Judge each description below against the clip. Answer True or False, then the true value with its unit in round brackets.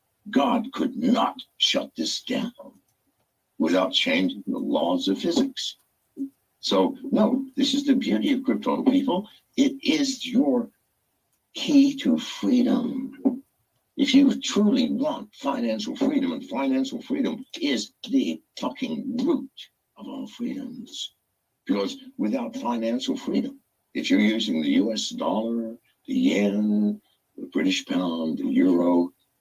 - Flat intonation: True (1.9 semitones)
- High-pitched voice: True (265 Hz)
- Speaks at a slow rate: True (120 wpm)